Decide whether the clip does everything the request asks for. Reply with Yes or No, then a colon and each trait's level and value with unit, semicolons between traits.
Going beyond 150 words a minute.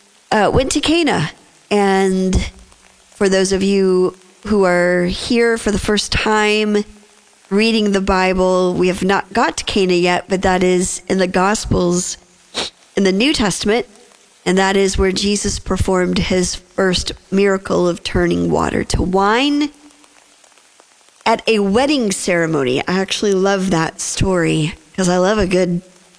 No: average, 145 wpm